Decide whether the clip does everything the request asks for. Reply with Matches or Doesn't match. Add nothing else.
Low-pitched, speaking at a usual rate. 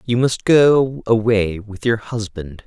Matches